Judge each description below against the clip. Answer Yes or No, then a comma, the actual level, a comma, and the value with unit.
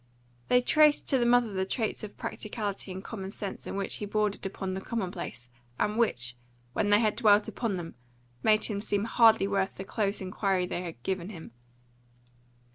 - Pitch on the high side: Yes, high, 205 Hz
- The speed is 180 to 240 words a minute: Yes, average, 185 wpm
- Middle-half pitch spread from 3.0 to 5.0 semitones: No, narrow, 2.5 semitones